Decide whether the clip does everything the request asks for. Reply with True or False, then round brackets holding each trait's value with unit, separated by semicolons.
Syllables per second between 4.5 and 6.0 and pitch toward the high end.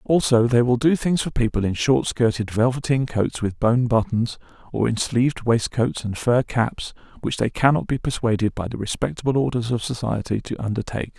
False (5.3 syllables/s; 120 Hz)